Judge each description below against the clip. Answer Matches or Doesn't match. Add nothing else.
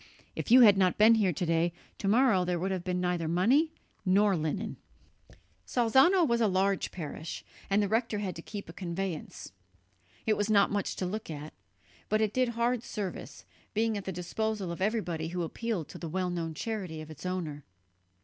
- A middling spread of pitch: Matches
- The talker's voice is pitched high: Matches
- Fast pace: Doesn't match